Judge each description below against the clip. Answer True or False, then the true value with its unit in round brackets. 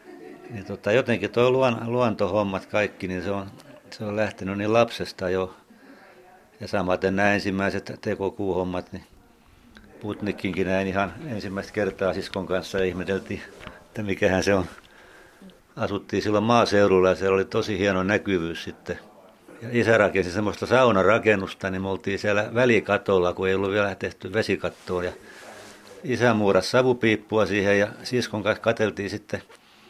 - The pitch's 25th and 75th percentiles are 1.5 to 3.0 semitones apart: True (2.7 semitones)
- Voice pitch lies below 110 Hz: True (100 Hz)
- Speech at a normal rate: True (135 wpm)